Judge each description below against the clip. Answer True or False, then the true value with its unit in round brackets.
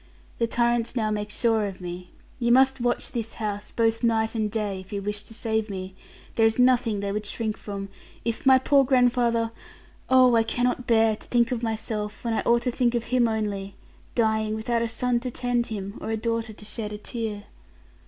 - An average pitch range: False (2.1 semitones)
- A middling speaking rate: False (210 wpm)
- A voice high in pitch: True (225 Hz)